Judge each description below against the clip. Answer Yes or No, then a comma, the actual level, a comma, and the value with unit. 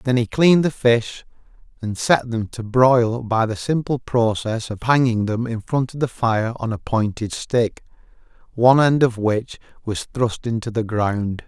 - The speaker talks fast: No, average, 185 wpm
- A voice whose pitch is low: Yes, low, 115 Hz